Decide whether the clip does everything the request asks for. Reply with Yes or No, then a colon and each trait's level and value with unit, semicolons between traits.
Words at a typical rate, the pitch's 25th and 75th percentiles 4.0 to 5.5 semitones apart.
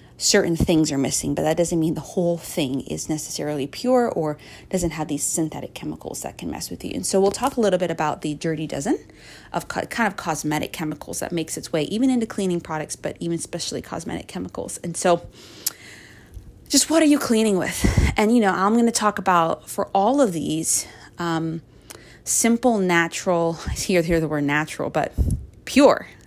Yes: average, 195 wpm; average, 4.5 semitones